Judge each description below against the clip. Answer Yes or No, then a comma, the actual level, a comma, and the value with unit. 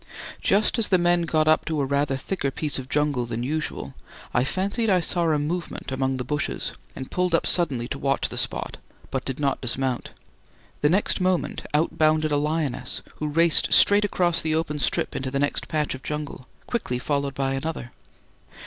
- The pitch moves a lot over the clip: No, average, 3.8 semitones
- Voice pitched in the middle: Yes, medium, 150 Hz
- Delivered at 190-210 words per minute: Yes, average, 195 wpm